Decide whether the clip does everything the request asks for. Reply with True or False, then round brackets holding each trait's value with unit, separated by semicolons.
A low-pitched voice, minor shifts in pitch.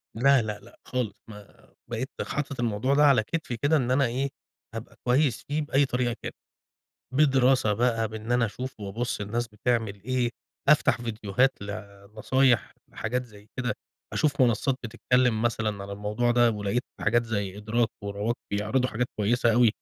False (120 Hz; 3.3 semitones)